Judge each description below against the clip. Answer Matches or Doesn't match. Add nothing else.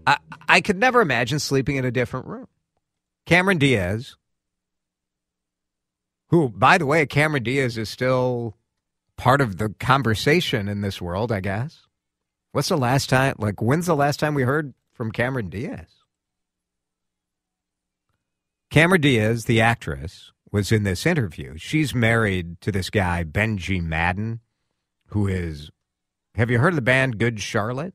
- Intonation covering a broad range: Matches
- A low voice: Matches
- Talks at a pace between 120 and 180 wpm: Matches